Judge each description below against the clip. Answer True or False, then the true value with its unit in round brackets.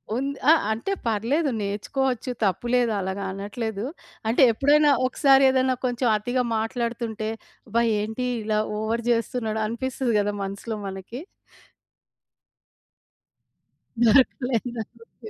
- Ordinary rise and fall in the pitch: True (3.0 semitones)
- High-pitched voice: True (230 Hz)